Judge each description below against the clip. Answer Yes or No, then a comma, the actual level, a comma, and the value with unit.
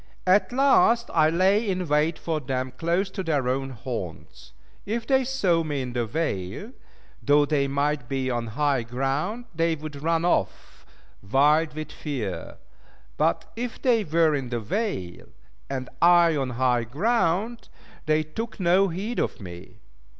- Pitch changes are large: Yes, wide, 6.2 semitones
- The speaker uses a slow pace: No, average, 155 wpm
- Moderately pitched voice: Yes, medium, 155 Hz